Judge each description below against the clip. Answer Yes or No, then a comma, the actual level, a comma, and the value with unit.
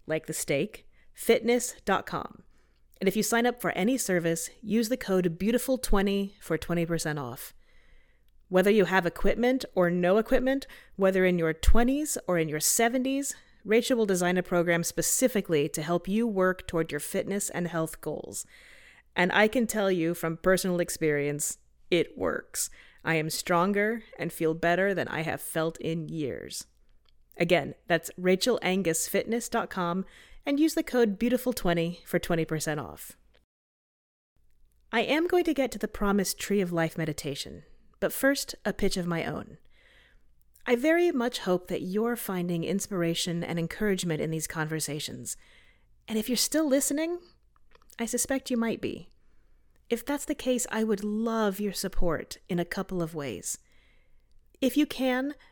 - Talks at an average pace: Yes, average, 155 wpm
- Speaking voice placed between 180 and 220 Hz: Yes, medium, 185 Hz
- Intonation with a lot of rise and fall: Yes, wide, 6.0 semitones